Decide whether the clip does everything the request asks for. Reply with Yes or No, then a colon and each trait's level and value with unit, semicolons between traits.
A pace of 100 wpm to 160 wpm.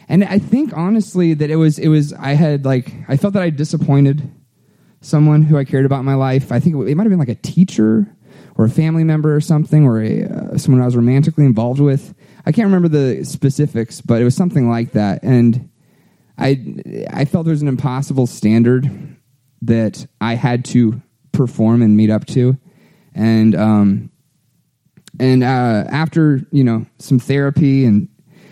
No: average, 185 wpm